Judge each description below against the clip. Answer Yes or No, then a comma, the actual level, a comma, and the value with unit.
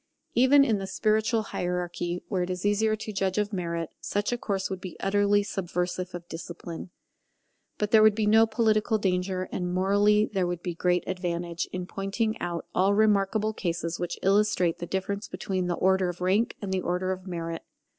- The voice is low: No, high, 190 Hz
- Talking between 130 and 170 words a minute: No, average, 185 wpm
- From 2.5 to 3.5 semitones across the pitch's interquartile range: Yes, average, 2.8 semitones